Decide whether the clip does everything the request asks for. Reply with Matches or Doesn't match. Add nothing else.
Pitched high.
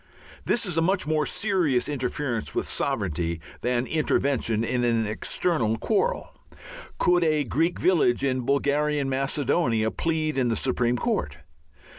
Doesn't match